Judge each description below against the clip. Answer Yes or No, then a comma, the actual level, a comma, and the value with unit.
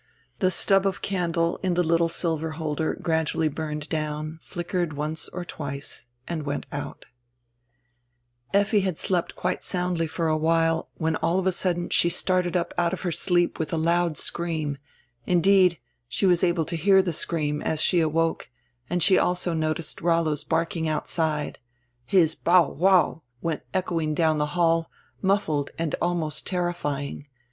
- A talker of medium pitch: Yes, medium, 165 Hz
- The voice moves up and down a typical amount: No, narrow, 2.2 semitones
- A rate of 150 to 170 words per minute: Yes, average, 160 wpm